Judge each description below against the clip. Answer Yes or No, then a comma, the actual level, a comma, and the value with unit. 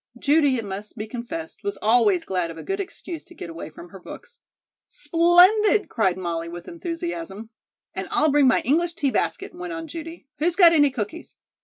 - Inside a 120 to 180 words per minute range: No, average, 190 wpm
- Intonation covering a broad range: Yes, wide, 8.5 semitones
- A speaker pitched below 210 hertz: No, very high, 295 Hz